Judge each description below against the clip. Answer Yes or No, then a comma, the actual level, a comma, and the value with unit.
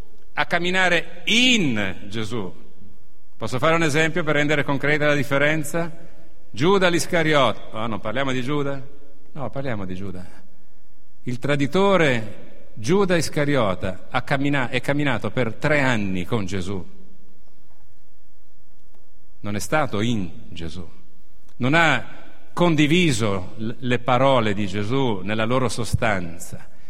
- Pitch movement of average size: No, wide, 6.6 semitones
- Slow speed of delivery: Yes, slow, 110 wpm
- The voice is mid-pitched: No, low, 130 Hz